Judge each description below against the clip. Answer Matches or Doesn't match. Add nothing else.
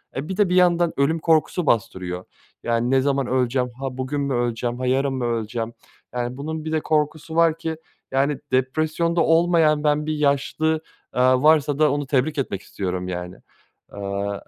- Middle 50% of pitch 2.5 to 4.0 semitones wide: Doesn't match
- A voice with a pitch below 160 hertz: Matches